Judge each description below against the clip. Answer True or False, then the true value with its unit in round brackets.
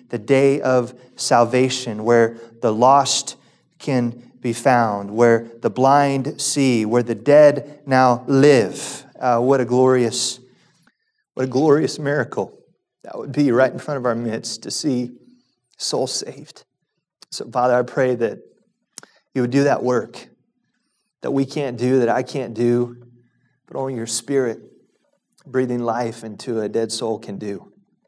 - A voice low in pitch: True (125 Hz)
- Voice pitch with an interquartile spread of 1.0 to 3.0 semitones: True (2.5 semitones)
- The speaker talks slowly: False (150 wpm)